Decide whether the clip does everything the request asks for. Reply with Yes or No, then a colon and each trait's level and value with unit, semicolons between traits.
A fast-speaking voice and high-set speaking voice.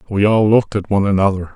No: fast, 230 wpm; low, 100 Hz